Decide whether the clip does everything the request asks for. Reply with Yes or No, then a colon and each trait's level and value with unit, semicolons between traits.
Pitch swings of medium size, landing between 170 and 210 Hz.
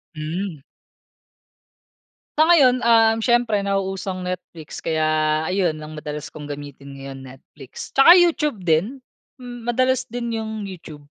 No: wide, 7.5 semitones; high, 190 Hz